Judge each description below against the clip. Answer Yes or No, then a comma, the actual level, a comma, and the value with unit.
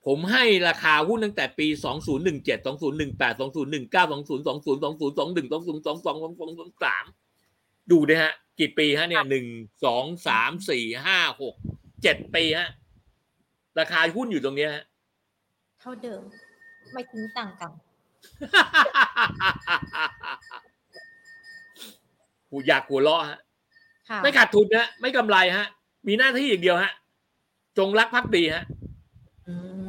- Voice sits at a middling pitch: Yes, medium, 180 Hz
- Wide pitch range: Yes, wide, 7.7 semitones